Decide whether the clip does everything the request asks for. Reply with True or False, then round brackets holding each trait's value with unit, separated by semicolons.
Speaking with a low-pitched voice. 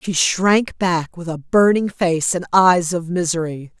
False (175 Hz)